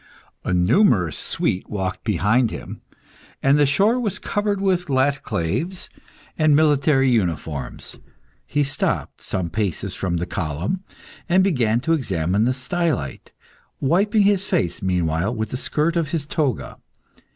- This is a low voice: Yes, low, 130 Hz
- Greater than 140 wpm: No, slow, 135 wpm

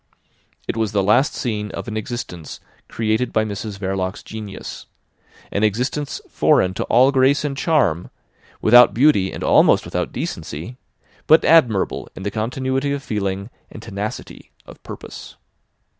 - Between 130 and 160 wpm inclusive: Yes, average, 145 wpm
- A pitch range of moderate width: Yes, average, 4.7 semitones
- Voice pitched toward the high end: No, low, 110 Hz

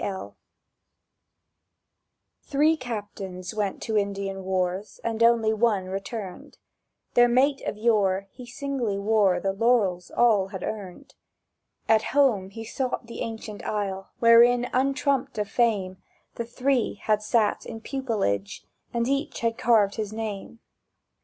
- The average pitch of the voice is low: No, high, 220 Hz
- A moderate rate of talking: No, slow, 130 wpm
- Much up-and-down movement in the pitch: No, average, 3.4 semitones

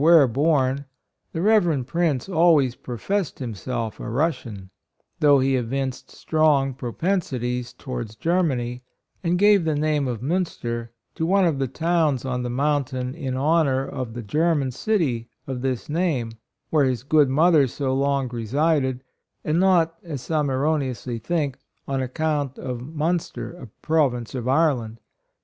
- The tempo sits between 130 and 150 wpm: Yes, average, 145 wpm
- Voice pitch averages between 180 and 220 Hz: No, medium, 140 Hz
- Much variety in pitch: No, average, 4.3 semitones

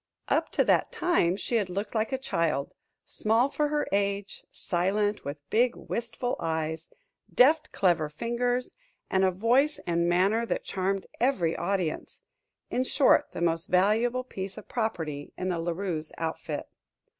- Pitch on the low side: No, high, 195 Hz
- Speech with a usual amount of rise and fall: No, wide, 5.8 semitones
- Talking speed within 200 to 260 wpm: No, average, 150 wpm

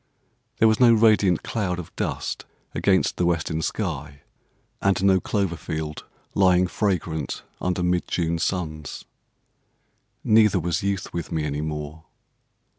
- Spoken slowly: Yes, slow, 130 wpm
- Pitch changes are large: No, average, 3.8 semitones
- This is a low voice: Yes, very low, 90 Hz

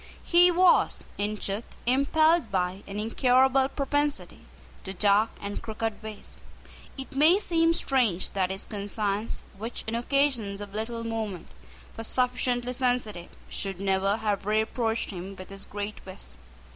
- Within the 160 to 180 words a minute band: No, average, 140 wpm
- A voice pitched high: Yes, high, 220 Hz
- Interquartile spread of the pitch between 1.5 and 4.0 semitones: No, average, 4.6 semitones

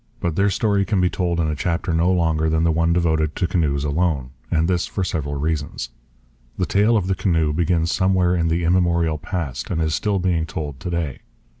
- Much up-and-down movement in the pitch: No, narrow, 2.5 semitones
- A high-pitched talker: No, very low, 85 Hz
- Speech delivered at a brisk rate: Yes, fast, 210 wpm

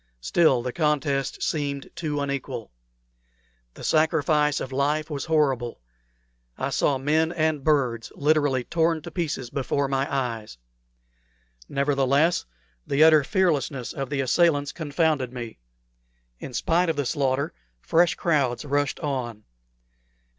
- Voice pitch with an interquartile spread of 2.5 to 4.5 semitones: Yes, average, 2.8 semitones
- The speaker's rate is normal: No, slow, 125 wpm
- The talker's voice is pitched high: No, medium, 145 Hz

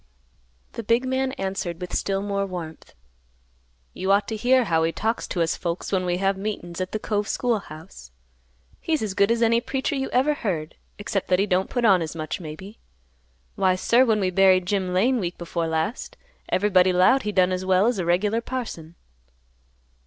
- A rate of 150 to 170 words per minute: No, average, 195 wpm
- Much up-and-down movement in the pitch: No, average, 4.0 semitones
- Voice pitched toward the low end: No, high, 195 Hz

